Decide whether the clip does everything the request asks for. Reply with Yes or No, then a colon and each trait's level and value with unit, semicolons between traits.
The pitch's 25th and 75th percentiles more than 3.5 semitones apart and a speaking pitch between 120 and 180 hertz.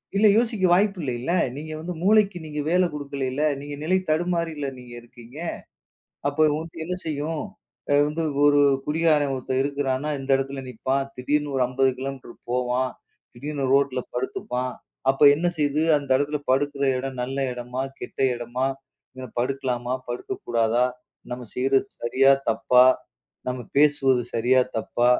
No: average, 3.1 semitones; low, 135 Hz